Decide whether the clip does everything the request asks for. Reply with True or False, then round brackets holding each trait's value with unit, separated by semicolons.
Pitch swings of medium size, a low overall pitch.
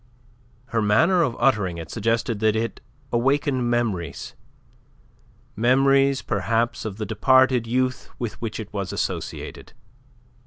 True (3.4 semitones; 115 Hz)